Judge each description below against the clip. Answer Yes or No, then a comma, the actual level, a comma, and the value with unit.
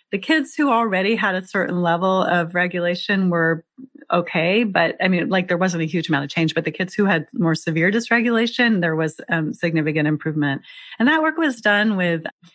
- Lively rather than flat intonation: No, average, 4.5 semitones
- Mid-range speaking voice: Yes, medium, 180 Hz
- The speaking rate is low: No, average, 200 wpm